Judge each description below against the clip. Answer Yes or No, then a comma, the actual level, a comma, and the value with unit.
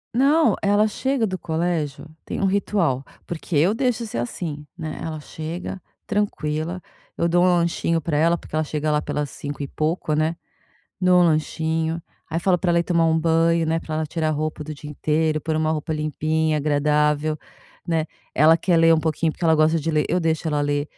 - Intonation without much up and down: Yes, narrow, 2.0 semitones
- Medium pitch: Yes, medium, 160 Hz